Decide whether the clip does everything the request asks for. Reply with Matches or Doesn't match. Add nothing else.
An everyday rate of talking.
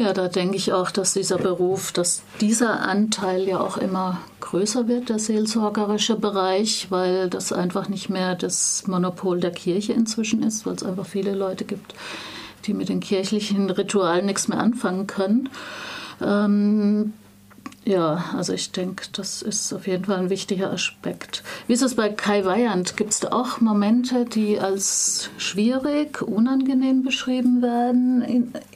Matches